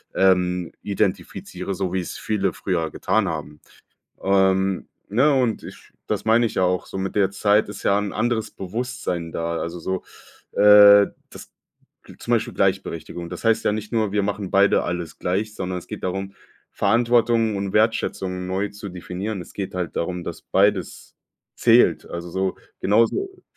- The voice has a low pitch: Yes, very low, 95 Hz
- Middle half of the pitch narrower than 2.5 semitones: No, average, 2.8 semitones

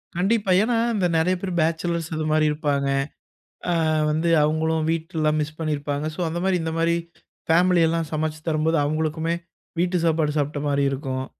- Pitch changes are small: Yes, narrow, 1.8 semitones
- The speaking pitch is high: No, medium, 160 Hz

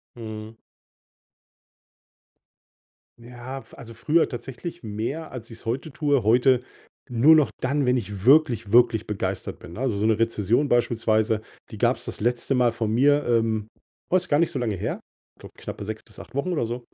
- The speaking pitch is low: Yes, low, 120 Hz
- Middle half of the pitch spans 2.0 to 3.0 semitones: No, average, 3.6 semitones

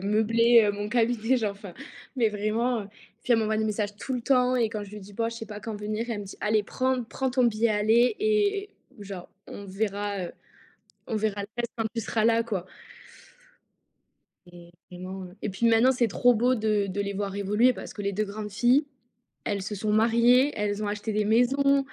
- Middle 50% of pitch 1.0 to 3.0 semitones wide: Yes, average, 2.7 semitones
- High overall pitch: Yes, high, 215 Hz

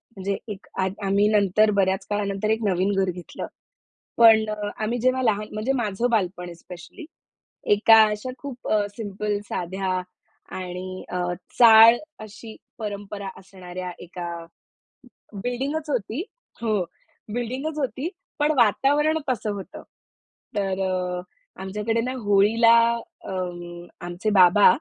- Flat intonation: No, average, 3.5 semitones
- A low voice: No, high, 205 Hz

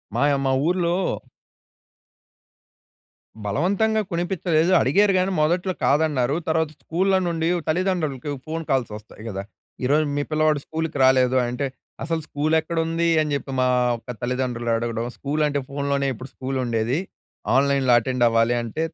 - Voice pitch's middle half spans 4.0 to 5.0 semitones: Yes, average, 4.3 semitones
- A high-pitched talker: No, medium, 145 Hz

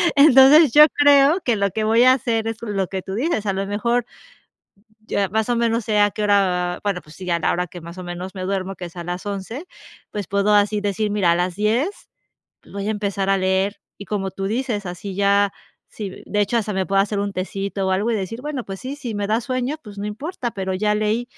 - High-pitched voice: Yes, high, 205 Hz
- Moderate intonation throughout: Yes, average, 3.2 semitones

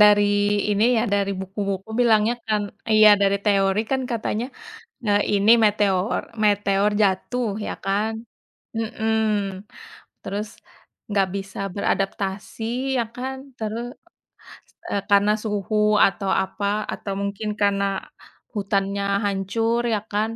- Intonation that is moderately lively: No, narrow, 1.8 semitones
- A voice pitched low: No, high, 205 Hz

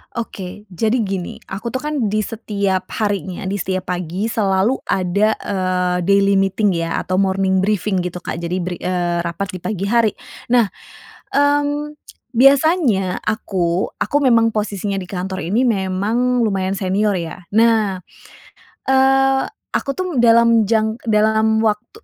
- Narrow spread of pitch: No, average, 3.7 semitones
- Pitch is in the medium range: No, high, 205 Hz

